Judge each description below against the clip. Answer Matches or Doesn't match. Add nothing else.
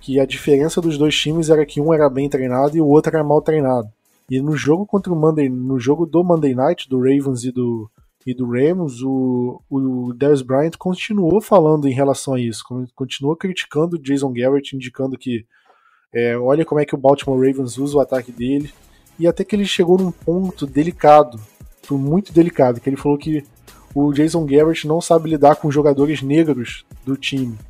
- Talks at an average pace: Doesn't match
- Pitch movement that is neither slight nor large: Matches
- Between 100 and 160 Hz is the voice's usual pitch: Matches